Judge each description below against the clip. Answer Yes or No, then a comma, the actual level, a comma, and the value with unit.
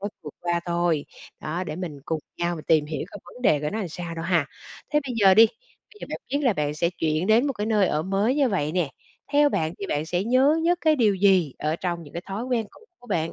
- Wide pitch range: Yes, wide, 5.8 semitones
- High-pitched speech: No, medium, 180 Hz